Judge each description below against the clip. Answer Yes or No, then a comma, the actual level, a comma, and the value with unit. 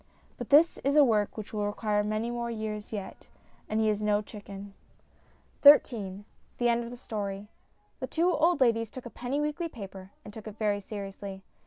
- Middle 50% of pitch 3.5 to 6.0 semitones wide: No, average, 3.0 semitones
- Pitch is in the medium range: No, high, 215 Hz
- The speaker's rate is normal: Yes, average, 190 wpm